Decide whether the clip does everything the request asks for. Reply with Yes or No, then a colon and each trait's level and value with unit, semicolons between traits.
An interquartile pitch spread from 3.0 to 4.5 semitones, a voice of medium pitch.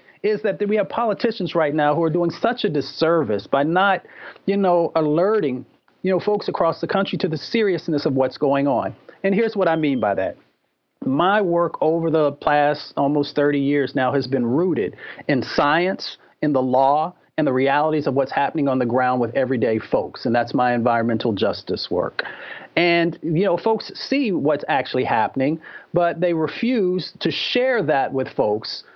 No: wide, 5.4 semitones; medium, 160 Hz